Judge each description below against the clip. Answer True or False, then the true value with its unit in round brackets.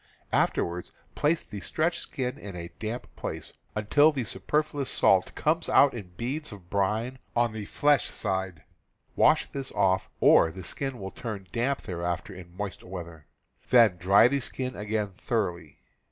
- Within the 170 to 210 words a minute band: False (155 wpm)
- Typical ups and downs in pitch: False (5.8 semitones)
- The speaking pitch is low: True (105 Hz)